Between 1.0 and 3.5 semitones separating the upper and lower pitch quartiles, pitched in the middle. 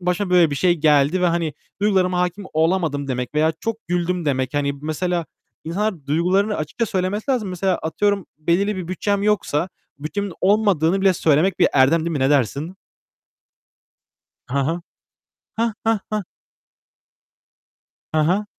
No: average, 4.4 semitones; medium, 175 Hz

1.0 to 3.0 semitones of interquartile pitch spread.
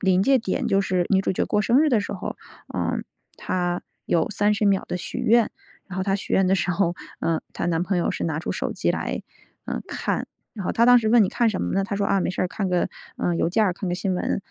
Yes: average, 2.7 semitones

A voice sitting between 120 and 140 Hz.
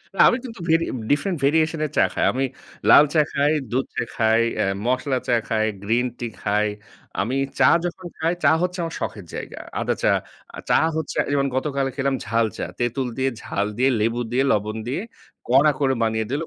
Yes: low, 135 Hz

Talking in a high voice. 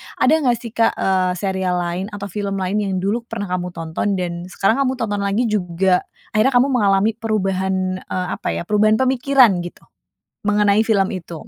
Yes: high, 200 Hz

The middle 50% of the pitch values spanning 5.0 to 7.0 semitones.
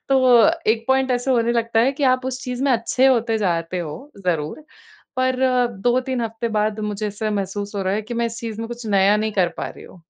No: average, 3.7 semitones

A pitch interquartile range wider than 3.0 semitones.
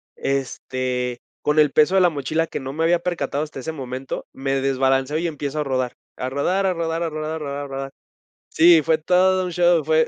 Yes: average, 3.6 semitones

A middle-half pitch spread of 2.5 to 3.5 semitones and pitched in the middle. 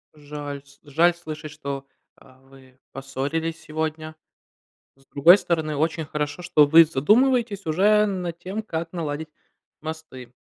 Yes: average, 3.1 semitones; medium, 155 Hz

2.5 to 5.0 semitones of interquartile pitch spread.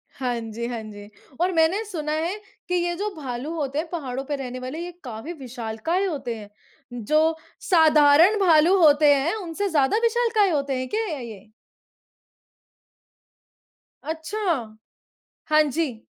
No: wide, 5.4 semitones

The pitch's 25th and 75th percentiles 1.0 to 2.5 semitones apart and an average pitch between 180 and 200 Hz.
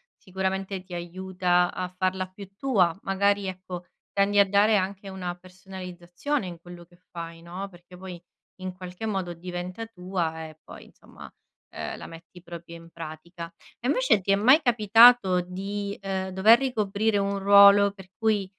Yes: narrow, 2.2 semitones; high, 190 Hz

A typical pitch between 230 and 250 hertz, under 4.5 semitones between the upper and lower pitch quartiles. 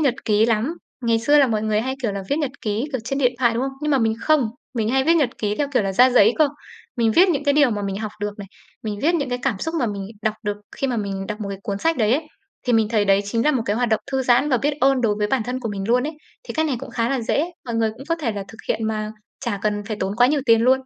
Yes: high, 235 Hz; average, 4.1 semitones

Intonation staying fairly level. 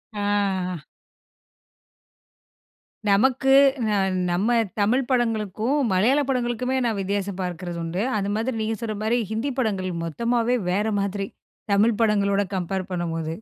No: average, 3.8 semitones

